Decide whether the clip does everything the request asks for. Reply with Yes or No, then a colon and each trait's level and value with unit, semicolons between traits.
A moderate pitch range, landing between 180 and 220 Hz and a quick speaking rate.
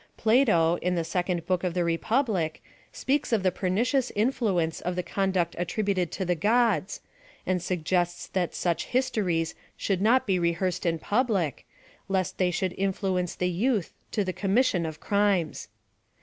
No: average, 3.2 semitones; medium, 185 Hz; average, 160 wpm